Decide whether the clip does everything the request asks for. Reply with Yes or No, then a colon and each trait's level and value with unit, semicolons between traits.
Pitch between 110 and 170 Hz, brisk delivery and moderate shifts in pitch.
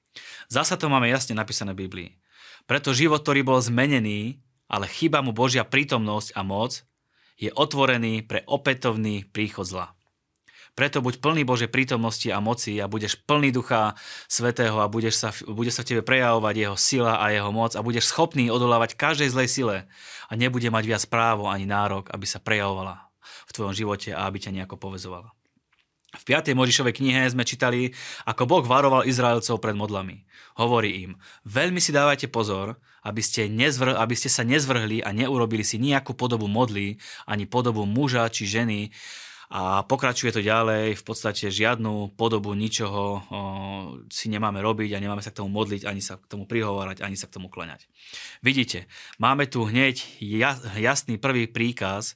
Yes: low, 115 Hz; fast, 170 wpm; average, 3.6 semitones